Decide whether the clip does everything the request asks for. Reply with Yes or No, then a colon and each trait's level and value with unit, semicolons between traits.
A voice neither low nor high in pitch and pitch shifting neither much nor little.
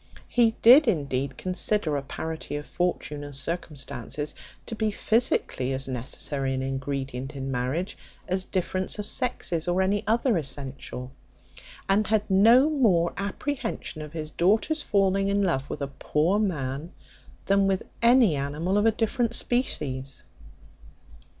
No: medium, 175 Hz; wide, 7.2 semitones